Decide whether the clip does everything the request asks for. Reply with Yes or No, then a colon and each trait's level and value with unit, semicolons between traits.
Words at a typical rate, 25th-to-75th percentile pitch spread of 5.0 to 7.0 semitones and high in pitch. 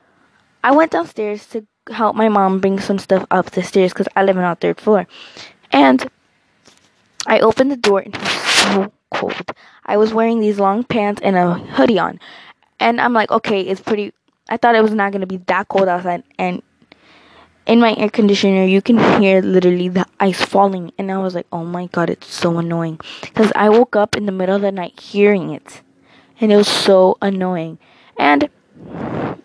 No: average, 195 wpm; narrow, 2.6 semitones; high, 200 Hz